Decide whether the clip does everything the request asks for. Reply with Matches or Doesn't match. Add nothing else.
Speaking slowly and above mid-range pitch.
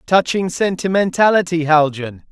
Doesn't match